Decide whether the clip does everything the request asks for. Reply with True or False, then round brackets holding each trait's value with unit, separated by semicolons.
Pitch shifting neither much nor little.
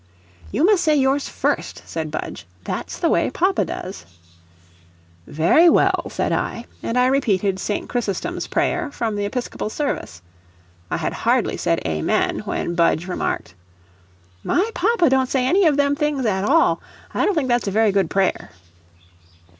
False (7.6 semitones)